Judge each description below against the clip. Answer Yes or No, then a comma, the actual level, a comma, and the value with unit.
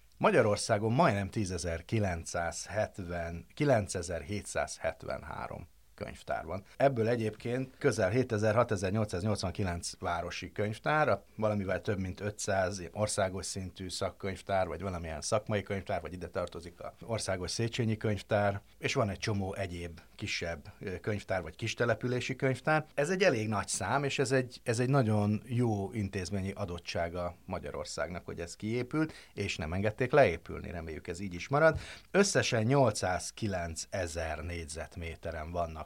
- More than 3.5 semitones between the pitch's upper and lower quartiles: Yes, average, 4.1 semitones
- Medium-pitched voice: No, low, 105 Hz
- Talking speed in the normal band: Yes, average, 115 wpm